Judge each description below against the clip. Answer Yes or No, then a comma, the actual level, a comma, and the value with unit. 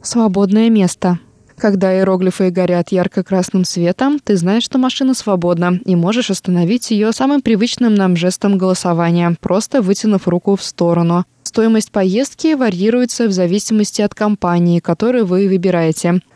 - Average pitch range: Yes, average, 3.7 semitones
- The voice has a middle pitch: No, high, 195 Hz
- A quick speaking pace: No, average, 130 wpm